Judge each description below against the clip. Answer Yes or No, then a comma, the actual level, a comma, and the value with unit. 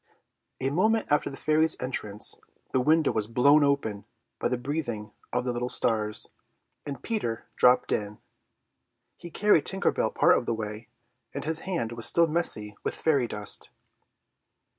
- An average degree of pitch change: No, wide, 5.9 semitones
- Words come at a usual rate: Yes, average, 165 wpm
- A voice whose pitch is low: Yes, low, 130 Hz